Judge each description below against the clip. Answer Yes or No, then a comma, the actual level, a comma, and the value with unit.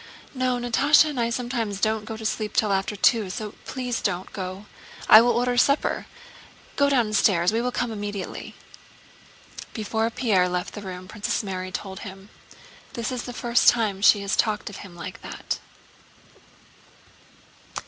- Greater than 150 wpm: Yes, average, 160 wpm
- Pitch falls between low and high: No, high, 215 Hz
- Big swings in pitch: No, average, 3.6 semitones